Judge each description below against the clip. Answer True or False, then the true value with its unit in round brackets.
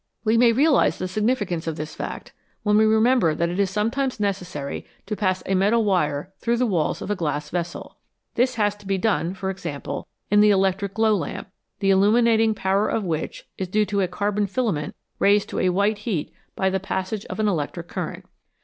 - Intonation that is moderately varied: True (3.1 semitones)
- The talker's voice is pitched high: True (200 Hz)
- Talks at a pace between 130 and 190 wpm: False (205 wpm)